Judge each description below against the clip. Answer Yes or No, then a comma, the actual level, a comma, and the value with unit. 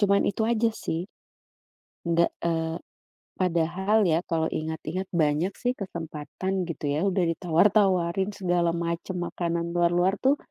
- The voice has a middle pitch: Yes, medium, 175 Hz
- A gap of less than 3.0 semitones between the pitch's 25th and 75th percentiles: Yes, narrow, 2.5 semitones